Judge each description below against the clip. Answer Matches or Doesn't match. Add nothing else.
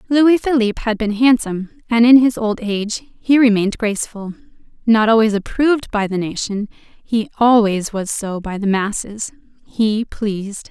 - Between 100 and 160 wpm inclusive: Matches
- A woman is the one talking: Matches